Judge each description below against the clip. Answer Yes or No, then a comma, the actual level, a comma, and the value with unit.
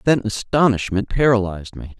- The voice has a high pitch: No, low, 110 Hz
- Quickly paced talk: No, slow, 120 wpm